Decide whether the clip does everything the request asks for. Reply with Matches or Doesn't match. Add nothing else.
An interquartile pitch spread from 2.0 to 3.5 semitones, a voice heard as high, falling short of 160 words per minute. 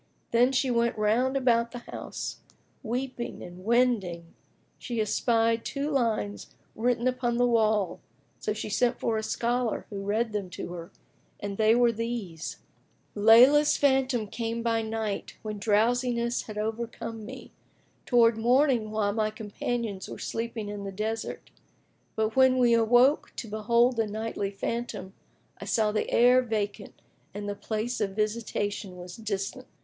Matches